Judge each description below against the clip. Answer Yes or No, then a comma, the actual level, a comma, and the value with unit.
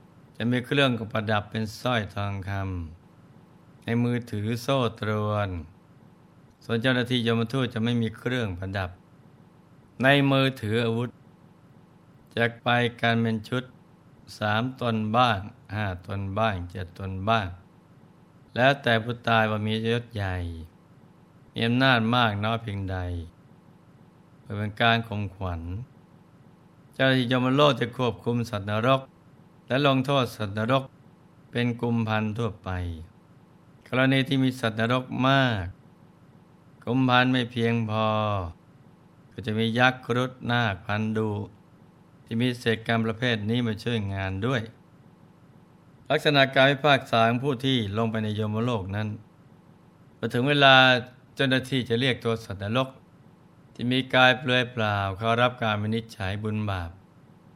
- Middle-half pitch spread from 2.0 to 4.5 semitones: Yes, average, 3.7 semitones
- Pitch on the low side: Yes, low, 120 Hz